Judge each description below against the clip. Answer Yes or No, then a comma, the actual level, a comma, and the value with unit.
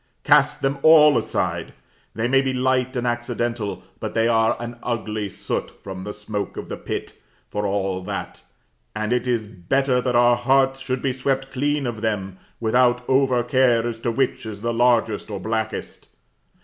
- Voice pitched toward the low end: Yes, low, 120 Hz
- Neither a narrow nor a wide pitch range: Yes, average, 3.0 semitones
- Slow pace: No, average, 175 wpm